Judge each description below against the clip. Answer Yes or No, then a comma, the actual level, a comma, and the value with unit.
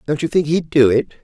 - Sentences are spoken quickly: Yes, fast, 290 wpm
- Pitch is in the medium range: Yes, medium, 150 Hz